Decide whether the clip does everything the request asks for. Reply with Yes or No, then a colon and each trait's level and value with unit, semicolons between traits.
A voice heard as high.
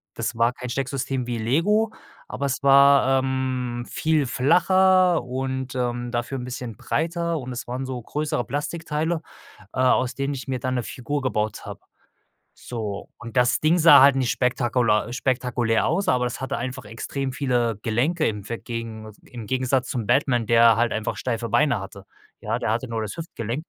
No: low, 125 Hz